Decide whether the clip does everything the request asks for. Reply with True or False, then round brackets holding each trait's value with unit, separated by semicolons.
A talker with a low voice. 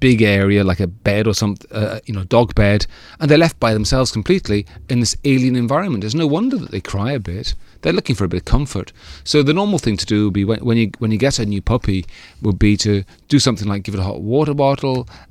True (110 Hz)